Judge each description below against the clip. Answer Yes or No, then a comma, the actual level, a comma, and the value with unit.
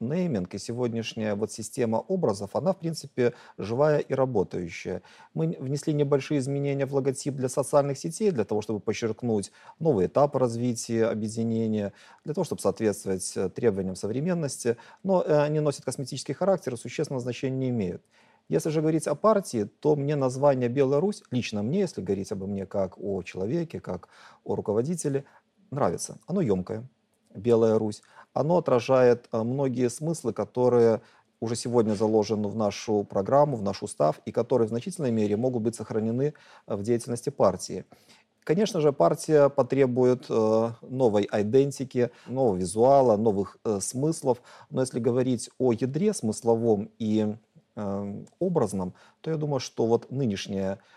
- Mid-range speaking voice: No, low, 125 Hz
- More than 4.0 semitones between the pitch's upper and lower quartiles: Yes, average, 4.6 semitones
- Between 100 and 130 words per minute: No, average, 140 wpm